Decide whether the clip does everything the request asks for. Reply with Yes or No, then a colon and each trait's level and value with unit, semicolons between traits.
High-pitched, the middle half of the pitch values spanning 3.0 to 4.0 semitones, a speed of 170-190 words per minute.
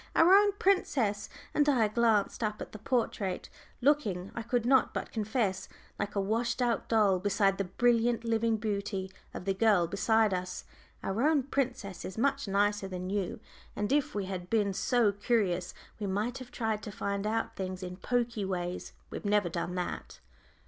Yes: high, 210 Hz; average, 3.6 semitones; average, 175 wpm